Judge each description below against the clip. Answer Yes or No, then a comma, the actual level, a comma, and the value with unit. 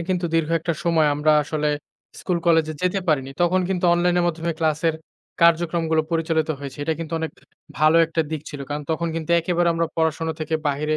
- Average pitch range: No, narrow, 1.6 semitones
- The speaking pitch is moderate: Yes, medium, 160 Hz